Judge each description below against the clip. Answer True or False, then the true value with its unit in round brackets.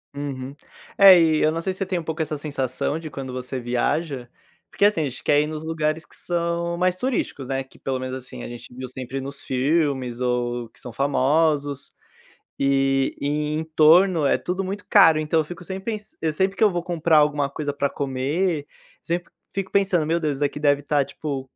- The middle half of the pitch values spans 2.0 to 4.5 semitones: True (3.9 semitones)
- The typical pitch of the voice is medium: True (150 Hz)